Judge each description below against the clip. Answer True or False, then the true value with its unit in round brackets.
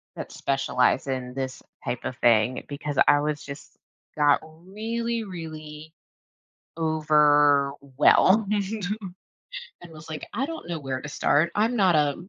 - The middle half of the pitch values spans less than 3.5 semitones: False (5.1 semitones)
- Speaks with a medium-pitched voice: True (150 Hz)